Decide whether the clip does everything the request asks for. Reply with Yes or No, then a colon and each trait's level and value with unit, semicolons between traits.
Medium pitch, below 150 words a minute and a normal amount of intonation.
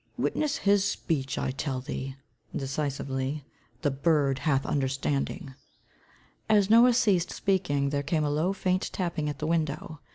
Yes: medium, 150 Hz; average, 140 wpm; average, 4.9 semitones